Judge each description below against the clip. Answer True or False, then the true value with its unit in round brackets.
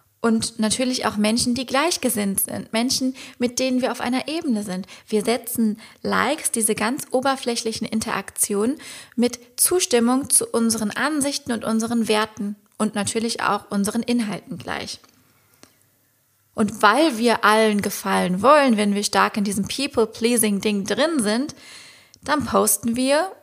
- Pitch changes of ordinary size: True (3.2 semitones)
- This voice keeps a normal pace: True (135 wpm)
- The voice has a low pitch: False (230 Hz)